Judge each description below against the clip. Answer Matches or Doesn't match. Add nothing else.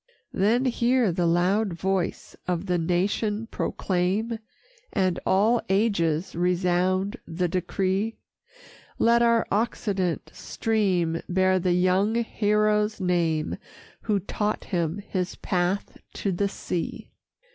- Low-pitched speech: Doesn't match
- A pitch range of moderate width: Matches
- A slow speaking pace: Matches